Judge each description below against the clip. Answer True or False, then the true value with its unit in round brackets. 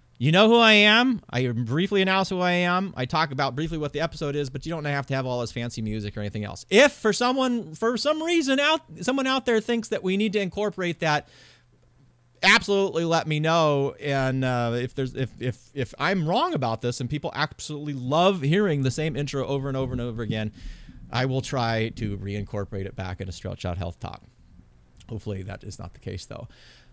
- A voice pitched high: False (140 Hz)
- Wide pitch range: True (7.8 semitones)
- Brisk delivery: True (220 wpm)